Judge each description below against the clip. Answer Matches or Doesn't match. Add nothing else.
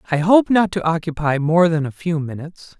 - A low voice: Doesn't match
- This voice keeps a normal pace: Doesn't match